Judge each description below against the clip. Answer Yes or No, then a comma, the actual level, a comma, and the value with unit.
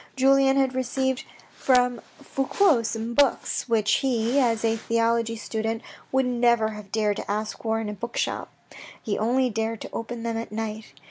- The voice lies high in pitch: Yes, high, 230 Hz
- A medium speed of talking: Yes, average, 170 wpm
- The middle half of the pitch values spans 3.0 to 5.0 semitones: No, narrow, 2.6 semitones